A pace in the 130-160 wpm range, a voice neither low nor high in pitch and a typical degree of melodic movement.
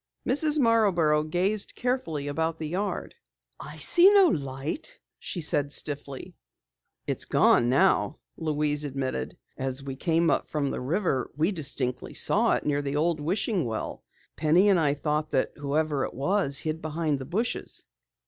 Yes: average, 155 wpm; medium, 155 Hz; average, 4.5 semitones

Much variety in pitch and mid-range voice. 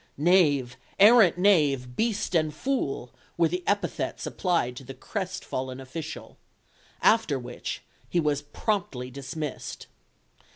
Yes: wide, 5.9 semitones; medium, 155 Hz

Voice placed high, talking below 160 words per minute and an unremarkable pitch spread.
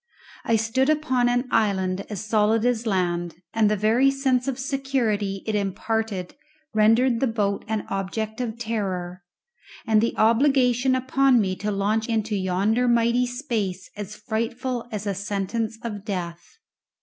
Yes: high, 220 Hz; average, 150 wpm; average, 3.4 semitones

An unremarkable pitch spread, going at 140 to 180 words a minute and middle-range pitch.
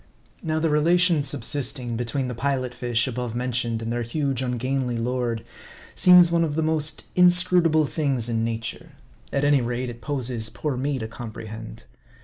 No: average, 4.2 semitones; average, 160 wpm; low, 130 Hz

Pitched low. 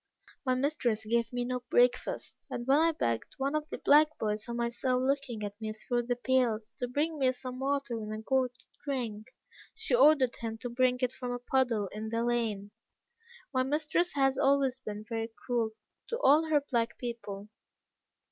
No: very high, 250 Hz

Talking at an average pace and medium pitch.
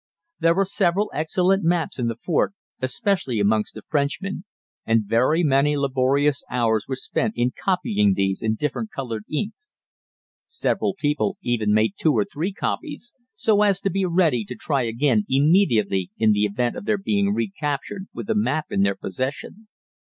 Yes: average, 165 wpm; medium, 145 Hz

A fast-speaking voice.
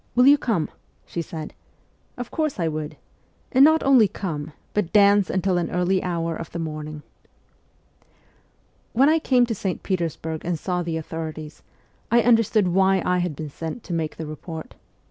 No: average, 175 wpm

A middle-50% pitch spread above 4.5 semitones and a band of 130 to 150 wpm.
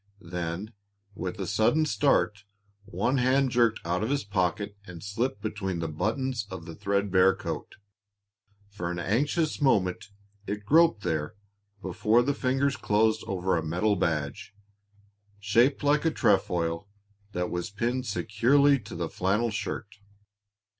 Yes: average, 5.2 semitones; average, 140 wpm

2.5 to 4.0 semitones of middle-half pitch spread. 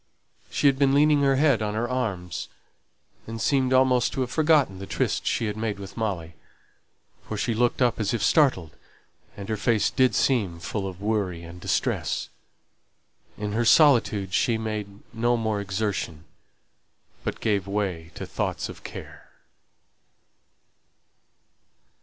No: average, 4.4 semitones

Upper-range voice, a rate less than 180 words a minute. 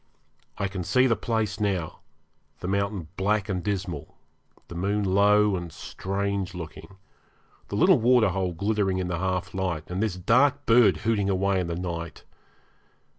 No: very low, 95 Hz; average, 155 wpm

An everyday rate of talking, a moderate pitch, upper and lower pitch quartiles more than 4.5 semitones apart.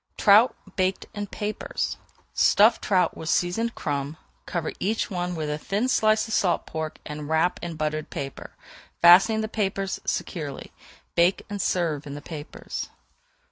Yes: average, 150 wpm; medium, 175 Hz; average, 4.9 semitones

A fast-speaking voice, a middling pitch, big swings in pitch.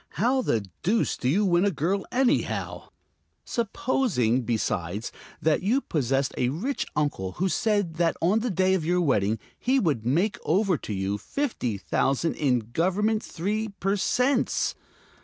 No: average, 155 wpm; medium, 175 Hz; wide, 8.8 semitones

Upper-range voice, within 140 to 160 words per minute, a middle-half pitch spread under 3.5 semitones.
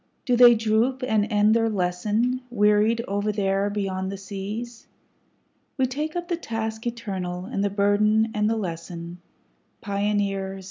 Yes: high, 210 Hz; average, 145 wpm; average, 2.8 semitones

